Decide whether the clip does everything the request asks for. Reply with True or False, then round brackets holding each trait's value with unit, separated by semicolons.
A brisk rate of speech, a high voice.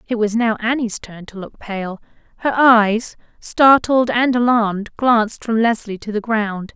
False (170 wpm; 225 Hz)